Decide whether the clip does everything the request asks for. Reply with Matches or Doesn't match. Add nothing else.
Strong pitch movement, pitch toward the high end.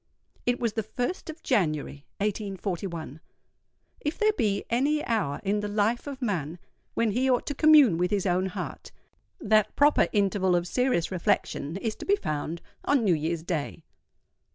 Matches